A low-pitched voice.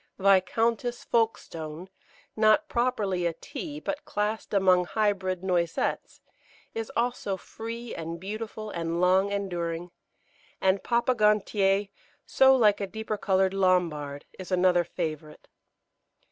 No: high, 195 Hz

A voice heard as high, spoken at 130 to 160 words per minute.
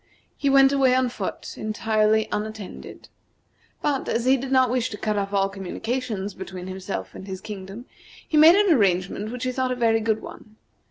No: high, 220 Hz; average, 185 wpm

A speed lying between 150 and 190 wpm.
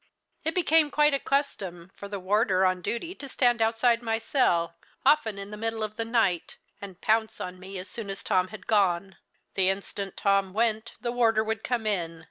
No: average, 200 wpm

